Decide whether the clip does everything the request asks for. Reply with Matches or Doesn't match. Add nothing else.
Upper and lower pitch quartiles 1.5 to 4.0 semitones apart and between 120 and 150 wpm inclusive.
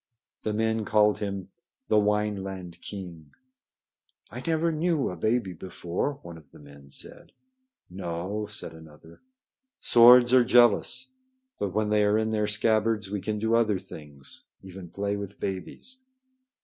Matches